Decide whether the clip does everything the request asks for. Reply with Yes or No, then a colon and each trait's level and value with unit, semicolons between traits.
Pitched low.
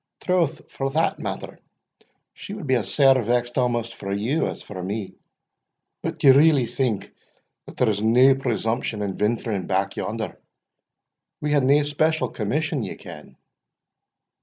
Yes: low, 125 Hz